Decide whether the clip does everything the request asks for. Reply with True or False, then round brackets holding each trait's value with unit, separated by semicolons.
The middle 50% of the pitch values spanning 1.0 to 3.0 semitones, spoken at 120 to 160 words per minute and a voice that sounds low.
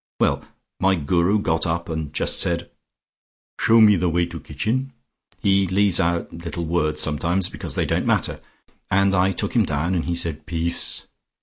False (2.6 semitones; 175 wpm; 85 Hz)